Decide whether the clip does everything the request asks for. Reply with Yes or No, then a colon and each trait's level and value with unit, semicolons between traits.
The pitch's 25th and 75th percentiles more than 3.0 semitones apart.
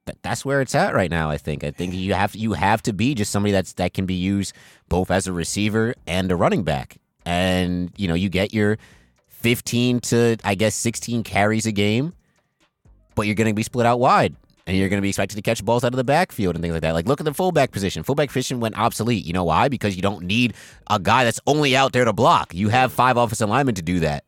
Yes: average, 4.6 semitones